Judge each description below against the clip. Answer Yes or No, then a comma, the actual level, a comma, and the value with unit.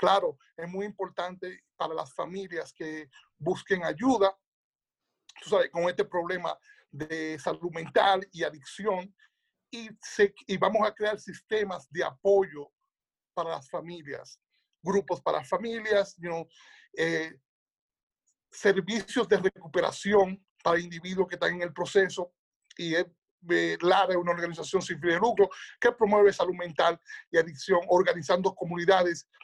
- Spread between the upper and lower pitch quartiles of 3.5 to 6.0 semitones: No, average, 3.0 semitones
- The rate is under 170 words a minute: Yes, slow, 135 wpm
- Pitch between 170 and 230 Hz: Yes, medium, 185 Hz